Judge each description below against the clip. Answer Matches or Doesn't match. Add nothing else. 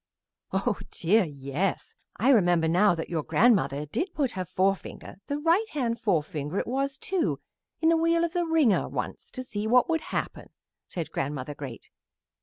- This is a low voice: Doesn't match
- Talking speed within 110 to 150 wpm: Doesn't match